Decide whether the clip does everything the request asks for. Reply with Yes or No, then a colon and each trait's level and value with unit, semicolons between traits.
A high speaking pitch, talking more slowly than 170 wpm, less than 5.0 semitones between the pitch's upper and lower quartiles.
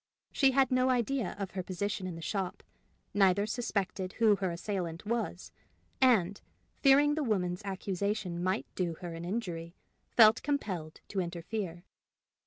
Yes: high, 195 Hz; average, 145 wpm; average, 4.1 semitones